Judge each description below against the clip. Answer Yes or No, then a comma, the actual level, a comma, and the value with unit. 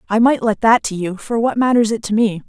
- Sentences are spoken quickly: Yes, fast, 290 wpm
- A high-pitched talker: Yes, high, 220 Hz